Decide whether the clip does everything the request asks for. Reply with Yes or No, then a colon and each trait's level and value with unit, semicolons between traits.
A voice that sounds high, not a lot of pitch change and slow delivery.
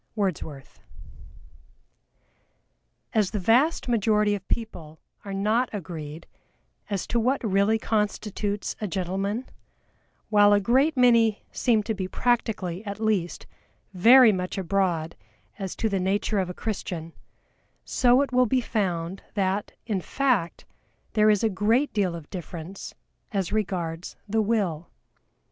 No: high, 205 Hz; average, 3.4 semitones; slow, 130 wpm